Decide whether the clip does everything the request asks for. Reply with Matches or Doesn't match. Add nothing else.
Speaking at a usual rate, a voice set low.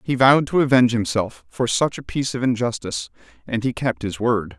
Doesn't match